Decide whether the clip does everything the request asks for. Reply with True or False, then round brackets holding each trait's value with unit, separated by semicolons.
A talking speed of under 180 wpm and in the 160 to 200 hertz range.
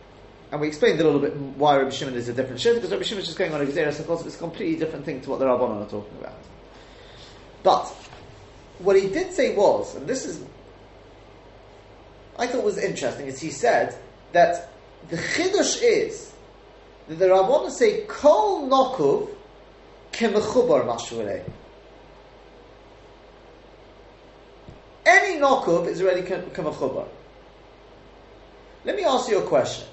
True (140 wpm; 185 Hz)